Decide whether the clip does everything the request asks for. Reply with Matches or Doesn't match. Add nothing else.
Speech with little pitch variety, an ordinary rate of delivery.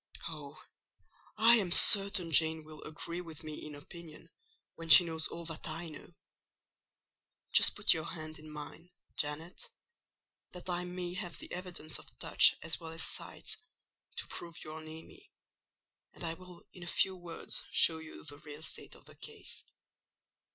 Matches